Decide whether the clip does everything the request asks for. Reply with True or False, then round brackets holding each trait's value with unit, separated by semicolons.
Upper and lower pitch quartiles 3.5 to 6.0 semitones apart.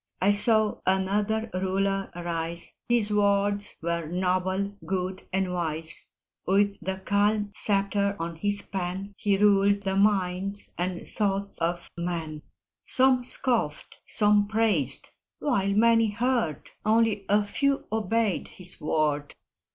False (2.5 semitones)